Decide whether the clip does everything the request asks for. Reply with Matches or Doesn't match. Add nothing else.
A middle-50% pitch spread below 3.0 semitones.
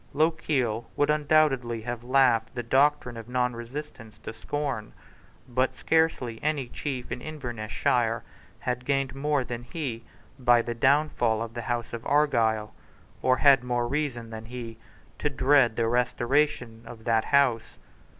Doesn't match